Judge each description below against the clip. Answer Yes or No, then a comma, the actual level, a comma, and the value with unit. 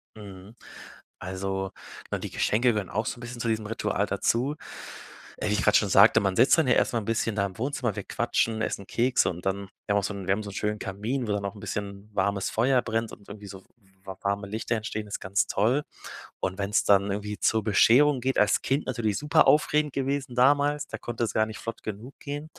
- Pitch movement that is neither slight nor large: Yes, average, 3.6 semitones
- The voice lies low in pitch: Yes, low, 110 Hz